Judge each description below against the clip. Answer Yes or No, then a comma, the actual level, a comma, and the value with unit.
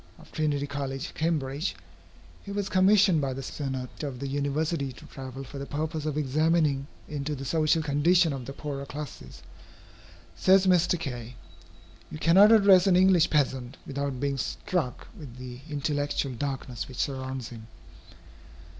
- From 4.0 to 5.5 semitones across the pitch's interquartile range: No, average, 3.4 semitones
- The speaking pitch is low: No, medium, 145 Hz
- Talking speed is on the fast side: No, average, 150 wpm